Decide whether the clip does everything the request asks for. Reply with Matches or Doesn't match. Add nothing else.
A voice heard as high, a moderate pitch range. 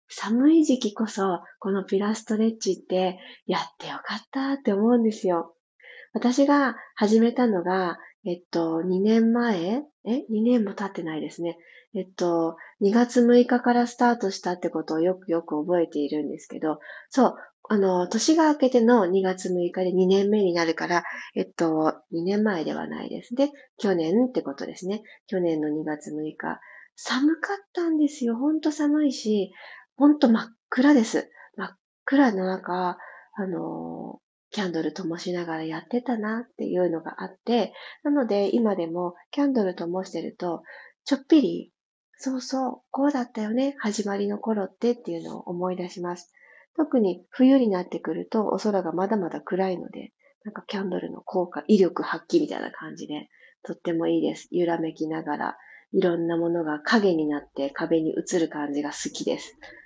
Doesn't match